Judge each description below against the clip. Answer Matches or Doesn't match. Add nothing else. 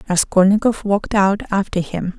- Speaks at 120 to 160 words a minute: Matches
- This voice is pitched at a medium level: Doesn't match